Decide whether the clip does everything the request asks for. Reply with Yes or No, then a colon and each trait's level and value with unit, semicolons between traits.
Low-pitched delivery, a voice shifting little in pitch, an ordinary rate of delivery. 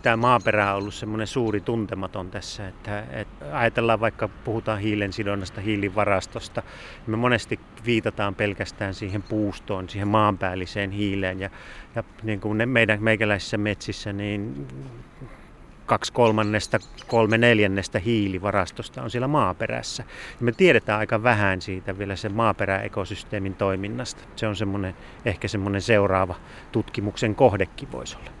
Yes: low, 105 Hz; narrow, 2.0 semitones; average, 130 wpm